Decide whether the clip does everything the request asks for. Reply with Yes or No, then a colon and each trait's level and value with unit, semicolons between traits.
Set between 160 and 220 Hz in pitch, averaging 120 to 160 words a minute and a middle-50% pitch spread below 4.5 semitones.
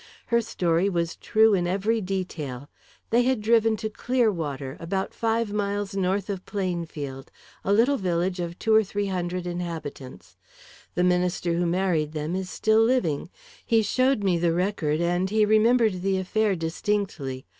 Yes: high, 190 Hz; average, 155 wpm; average, 4.0 semitones